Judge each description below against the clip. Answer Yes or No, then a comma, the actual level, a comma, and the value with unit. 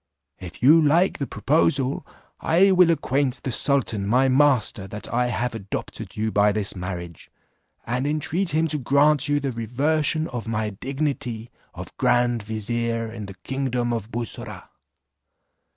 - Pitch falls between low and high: No, low, 125 Hz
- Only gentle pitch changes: No, average, 4.7 semitones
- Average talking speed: Yes, average, 150 wpm